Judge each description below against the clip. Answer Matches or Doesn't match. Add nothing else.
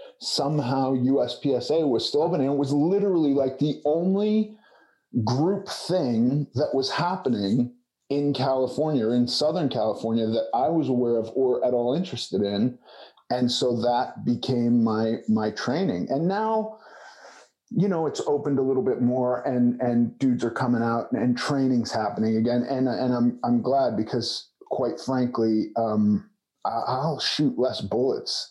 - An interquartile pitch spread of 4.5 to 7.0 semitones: Doesn't match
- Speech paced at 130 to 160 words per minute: Matches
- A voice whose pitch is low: Matches